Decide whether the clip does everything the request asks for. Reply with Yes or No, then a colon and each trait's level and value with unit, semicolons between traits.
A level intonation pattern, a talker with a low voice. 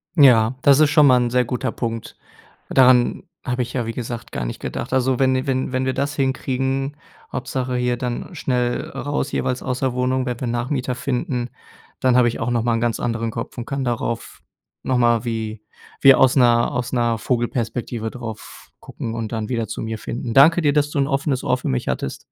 Yes: narrow, 2.0 semitones; low, 125 Hz